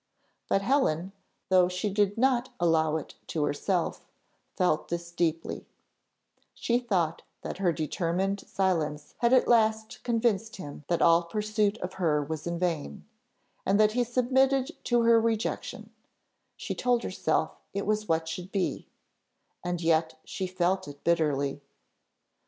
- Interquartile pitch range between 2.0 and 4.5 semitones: No, average, 5.2 semitones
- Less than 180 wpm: Yes, average, 140 wpm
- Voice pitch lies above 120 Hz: Yes, medium, 185 Hz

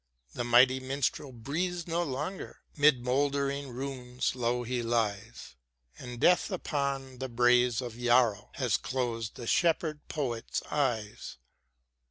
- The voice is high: No, low, 130 Hz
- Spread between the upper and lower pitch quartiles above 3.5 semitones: No, average, 2.9 semitones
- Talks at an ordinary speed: No, slow, 125 wpm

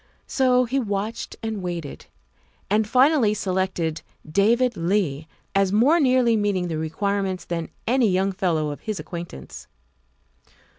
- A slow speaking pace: Yes, slow, 130 wpm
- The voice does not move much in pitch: No, average, 4.9 semitones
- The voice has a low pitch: No, high, 200 Hz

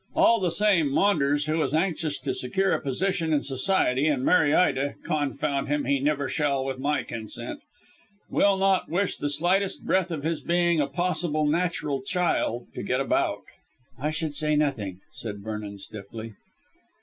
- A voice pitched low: No, medium, 150 Hz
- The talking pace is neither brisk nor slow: Yes, average, 165 wpm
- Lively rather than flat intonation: No, average, 4.3 semitones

